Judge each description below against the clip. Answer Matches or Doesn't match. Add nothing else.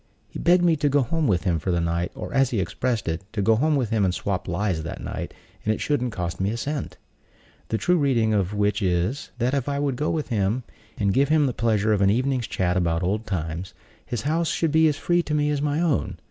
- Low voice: Matches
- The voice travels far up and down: Matches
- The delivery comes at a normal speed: Doesn't match